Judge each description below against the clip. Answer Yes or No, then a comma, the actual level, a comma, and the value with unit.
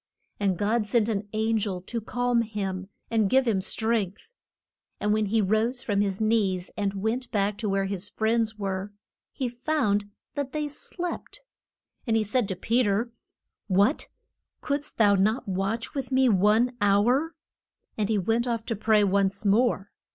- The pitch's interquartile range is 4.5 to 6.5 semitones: No, average, 3.0 semitones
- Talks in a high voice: Yes, high, 215 Hz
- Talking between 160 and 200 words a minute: Yes, average, 165 wpm